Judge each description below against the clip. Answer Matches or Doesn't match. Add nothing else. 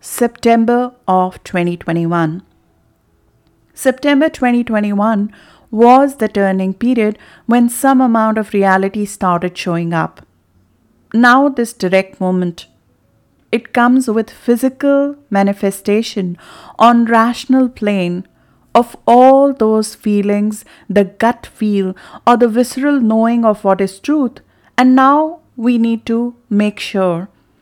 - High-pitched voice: Matches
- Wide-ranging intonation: Doesn't match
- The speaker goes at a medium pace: Doesn't match